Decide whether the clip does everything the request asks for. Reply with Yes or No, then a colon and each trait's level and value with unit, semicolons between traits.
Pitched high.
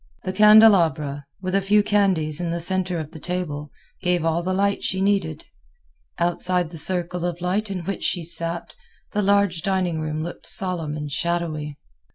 No: medium, 175 Hz